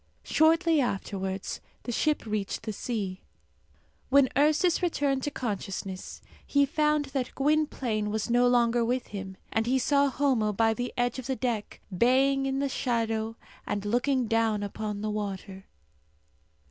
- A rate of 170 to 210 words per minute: No, average, 145 wpm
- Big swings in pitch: No, average, 4.5 semitones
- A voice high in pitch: Yes, high, 240 Hz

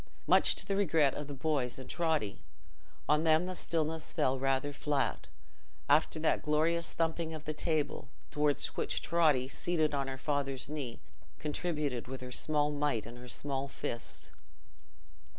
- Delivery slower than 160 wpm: Yes, average, 150 wpm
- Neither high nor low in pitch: Yes, medium, 150 Hz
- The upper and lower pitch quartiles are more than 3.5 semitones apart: No, average, 2.8 semitones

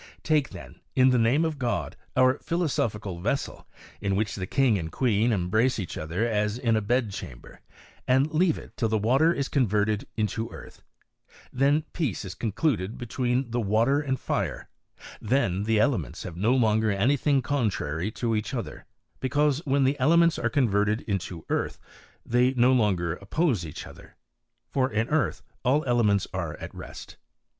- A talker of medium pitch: No, low, 115 Hz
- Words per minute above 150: Yes, average, 170 wpm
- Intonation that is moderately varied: Yes, average, 4.6 semitones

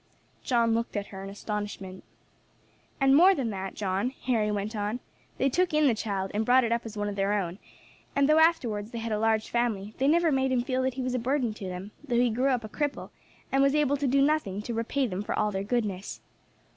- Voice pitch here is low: No, high, 230 Hz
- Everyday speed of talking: No, fast, 240 wpm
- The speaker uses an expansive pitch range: No, average, 4.5 semitones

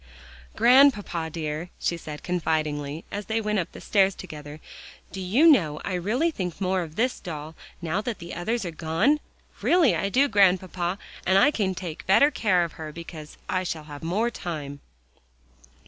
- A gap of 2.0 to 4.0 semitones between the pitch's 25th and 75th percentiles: No, average, 4.8 semitones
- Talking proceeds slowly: No, average, 175 wpm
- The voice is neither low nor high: Yes, medium, 180 Hz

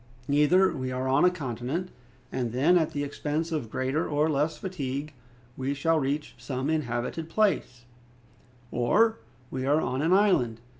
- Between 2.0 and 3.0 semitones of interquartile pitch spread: No, average, 3.9 semitones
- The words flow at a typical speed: Yes, average, 155 wpm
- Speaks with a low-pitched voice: No, medium, 145 Hz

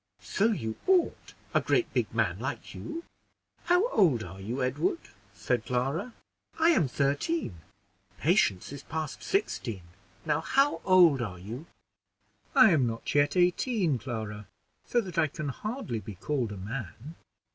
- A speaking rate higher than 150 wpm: No, average, 145 wpm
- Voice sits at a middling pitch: Yes, medium, 145 Hz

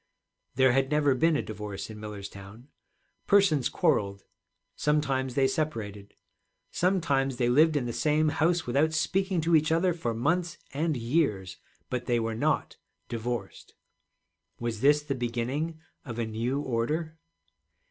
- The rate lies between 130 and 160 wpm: Yes, average, 140 wpm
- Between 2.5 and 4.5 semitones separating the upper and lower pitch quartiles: No, average, 5.2 semitones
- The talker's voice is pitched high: No, low, 135 Hz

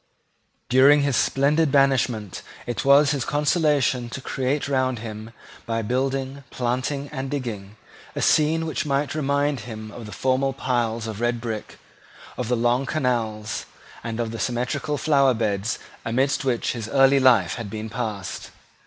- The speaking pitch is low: Yes, low, 130 Hz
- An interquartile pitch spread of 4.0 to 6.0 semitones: No, average, 3.4 semitones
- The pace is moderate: Yes, average, 155 wpm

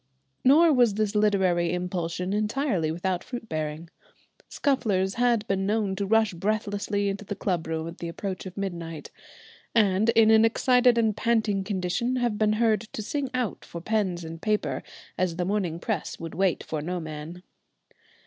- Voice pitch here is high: Yes, high, 200 Hz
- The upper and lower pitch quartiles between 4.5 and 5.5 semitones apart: No, average, 4.0 semitones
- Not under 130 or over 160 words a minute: No, average, 170 wpm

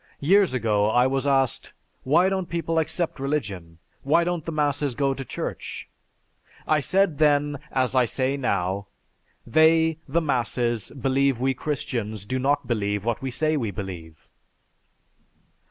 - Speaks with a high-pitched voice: No, low, 135 Hz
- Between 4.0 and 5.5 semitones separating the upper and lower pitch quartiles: Yes, average, 4.6 semitones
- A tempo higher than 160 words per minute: No, average, 145 wpm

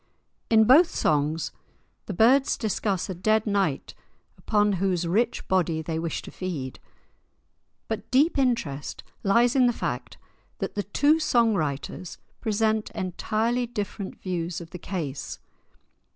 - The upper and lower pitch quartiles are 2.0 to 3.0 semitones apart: No, average, 5.2 semitones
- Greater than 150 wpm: No, slow, 135 wpm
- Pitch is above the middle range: Yes, high, 200 Hz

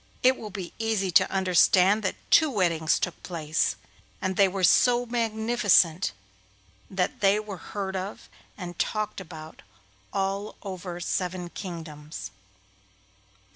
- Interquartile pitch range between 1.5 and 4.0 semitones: Yes, average, 3.2 semitones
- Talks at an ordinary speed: No, slow, 125 wpm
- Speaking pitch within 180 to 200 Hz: Yes, high, 190 Hz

